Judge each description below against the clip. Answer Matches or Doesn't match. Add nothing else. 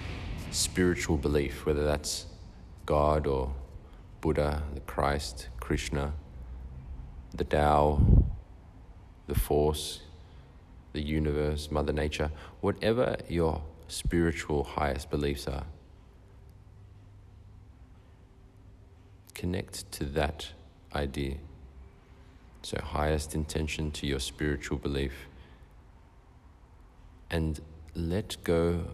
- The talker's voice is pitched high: Doesn't match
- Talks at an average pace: Doesn't match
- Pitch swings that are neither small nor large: Matches